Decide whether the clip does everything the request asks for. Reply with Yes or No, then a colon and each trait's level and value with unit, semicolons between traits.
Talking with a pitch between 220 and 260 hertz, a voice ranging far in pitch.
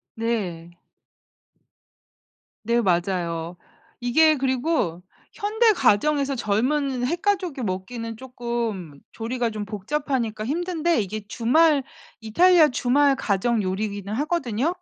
Yes: high, 240 Hz; wide, 6.2 semitones